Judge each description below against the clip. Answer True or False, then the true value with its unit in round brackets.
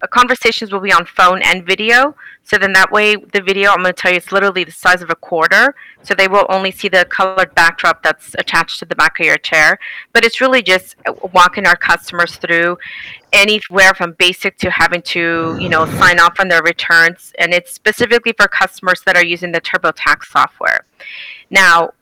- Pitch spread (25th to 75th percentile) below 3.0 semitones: True (2.6 semitones)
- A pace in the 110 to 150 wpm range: False (200 wpm)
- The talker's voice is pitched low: False (185 Hz)